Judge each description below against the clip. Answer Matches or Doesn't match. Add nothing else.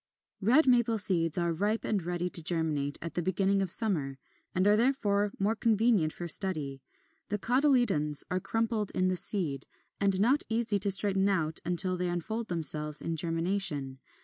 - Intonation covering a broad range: Doesn't match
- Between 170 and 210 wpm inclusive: Matches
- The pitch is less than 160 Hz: Doesn't match